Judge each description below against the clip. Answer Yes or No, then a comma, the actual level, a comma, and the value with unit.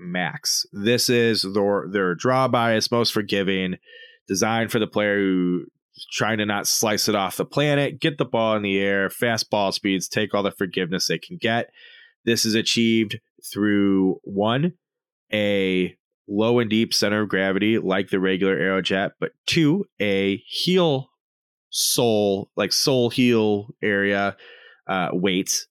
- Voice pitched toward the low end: Yes, low, 105 Hz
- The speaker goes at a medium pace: Yes, average, 150 wpm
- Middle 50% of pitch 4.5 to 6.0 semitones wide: No, average, 3.3 semitones